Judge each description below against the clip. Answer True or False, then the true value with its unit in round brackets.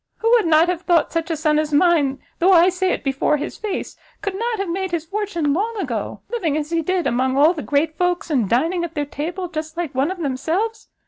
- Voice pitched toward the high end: True (335 Hz)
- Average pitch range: True (3.8 semitones)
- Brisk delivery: True (240 wpm)